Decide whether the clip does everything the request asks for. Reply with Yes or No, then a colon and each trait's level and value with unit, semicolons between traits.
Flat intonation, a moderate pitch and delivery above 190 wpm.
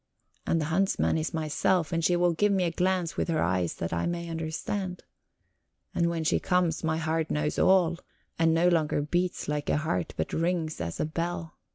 Yes: narrow, 2.1 semitones; medium, 165 Hz; average, 200 wpm